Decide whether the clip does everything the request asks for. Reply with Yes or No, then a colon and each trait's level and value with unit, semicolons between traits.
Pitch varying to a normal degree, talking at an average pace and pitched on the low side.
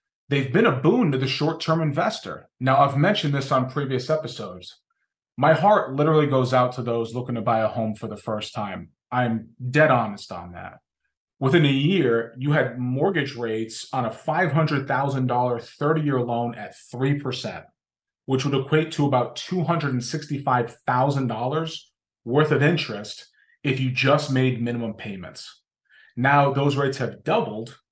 Yes: average, 3.8 semitones; average, 155 wpm; low, 130 Hz